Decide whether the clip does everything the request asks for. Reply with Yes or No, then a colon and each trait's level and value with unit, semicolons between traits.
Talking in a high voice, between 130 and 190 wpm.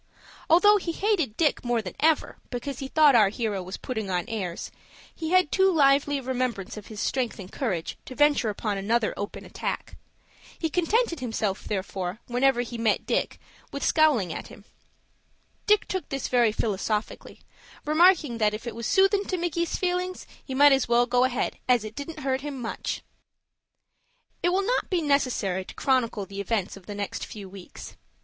Yes: very high, 250 Hz; average, 175 wpm